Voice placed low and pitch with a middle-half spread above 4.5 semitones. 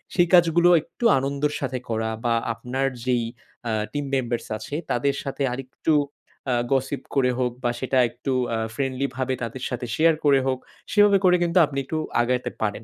No: low, 130 Hz; average, 2.9 semitones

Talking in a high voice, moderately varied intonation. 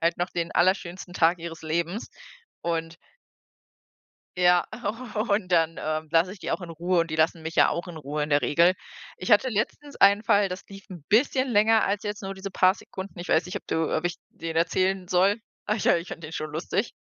No: medium, 180 Hz; average, 3.1 semitones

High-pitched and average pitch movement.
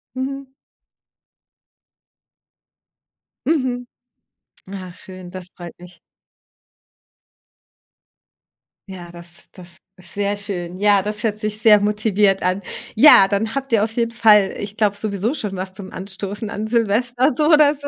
Yes: high, 205 Hz; average, 3.5 semitones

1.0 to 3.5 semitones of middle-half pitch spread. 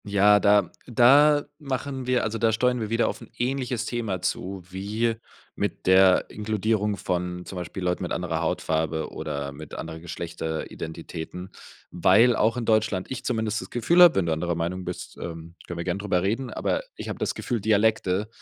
No: average, 4.6 semitones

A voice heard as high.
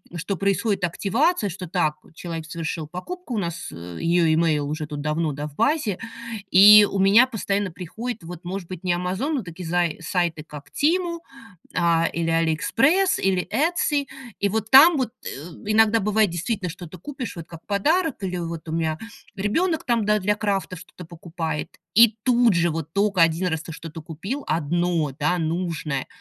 No: medium, 180 Hz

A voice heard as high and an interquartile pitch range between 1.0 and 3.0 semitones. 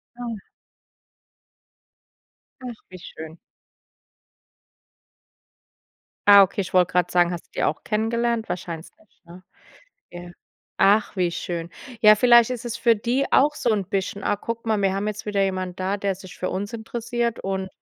No: high, 200 Hz; average, 4.0 semitones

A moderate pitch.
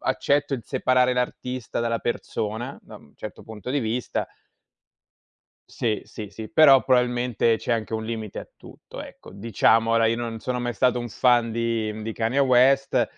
No: low, 120 Hz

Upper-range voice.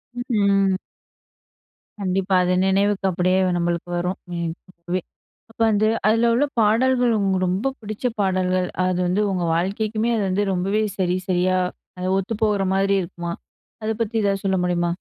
Yes: high, 195 Hz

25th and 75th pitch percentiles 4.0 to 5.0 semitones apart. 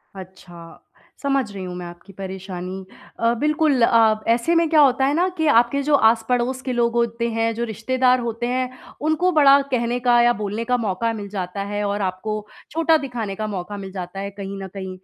Yes: average, 4.6 semitones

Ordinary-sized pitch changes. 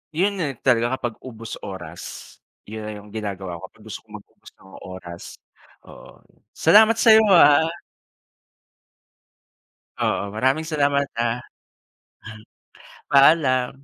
No: wide, 5.9 semitones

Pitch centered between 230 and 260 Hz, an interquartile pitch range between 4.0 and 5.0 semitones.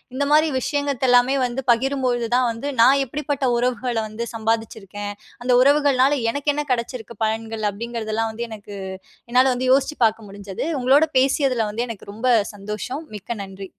No: high, 240 Hz; average, 3.4 semitones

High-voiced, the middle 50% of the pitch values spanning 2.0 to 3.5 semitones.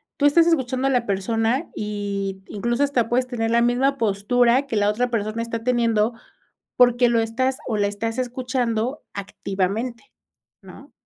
Yes: high, 235 Hz; average, 3.0 semitones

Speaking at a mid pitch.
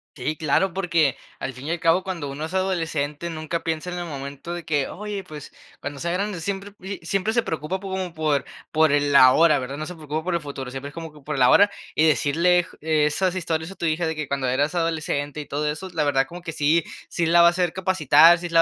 Yes: medium, 160 Hz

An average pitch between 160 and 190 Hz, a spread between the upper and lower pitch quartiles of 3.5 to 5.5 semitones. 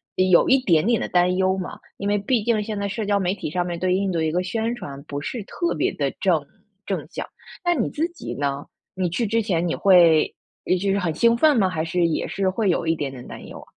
Yes: medium, 185 Hz; average, 4.2 semitones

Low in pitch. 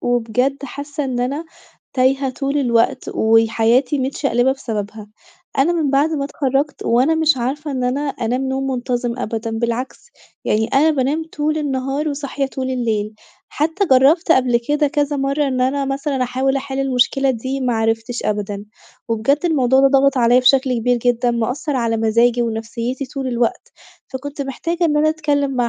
No: very high, 265 Hz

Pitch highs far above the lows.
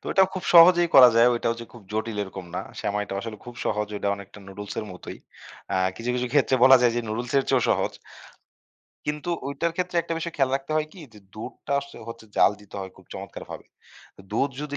Yes: wide, 5.7 semitones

